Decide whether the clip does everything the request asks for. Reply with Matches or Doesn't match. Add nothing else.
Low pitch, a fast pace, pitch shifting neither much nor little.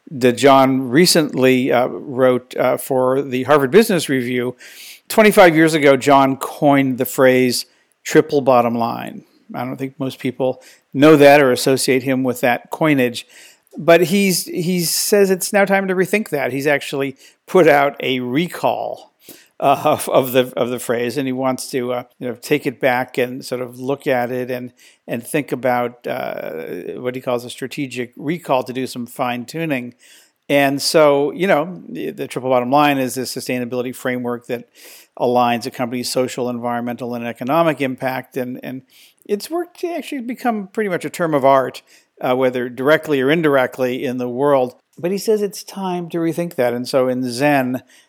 Doesn't match